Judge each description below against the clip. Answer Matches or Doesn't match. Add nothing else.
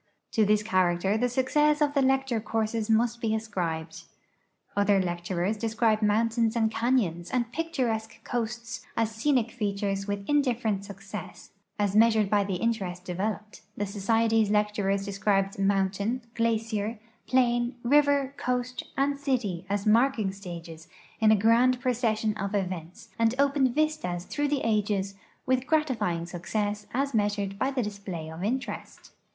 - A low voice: Doesn't match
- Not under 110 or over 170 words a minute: Matches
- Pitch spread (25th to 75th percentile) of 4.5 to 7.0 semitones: Doesn't match